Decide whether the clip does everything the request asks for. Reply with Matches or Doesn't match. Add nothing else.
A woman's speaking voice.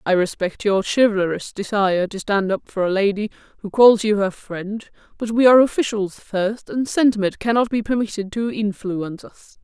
Matches